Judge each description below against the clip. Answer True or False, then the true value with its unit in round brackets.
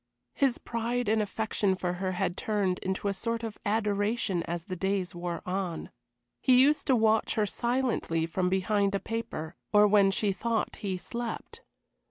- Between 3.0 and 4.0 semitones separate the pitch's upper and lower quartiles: True (3.4 semitones)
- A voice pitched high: True (205 Hz)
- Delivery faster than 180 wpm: False (170 wpm)